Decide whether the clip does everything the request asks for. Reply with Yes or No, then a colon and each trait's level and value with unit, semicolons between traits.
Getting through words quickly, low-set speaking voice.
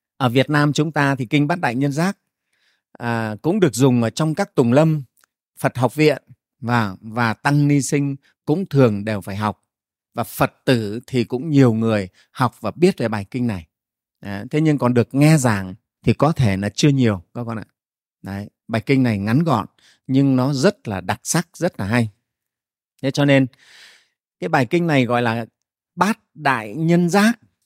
No: average, 195 wpm; low, 130 Hz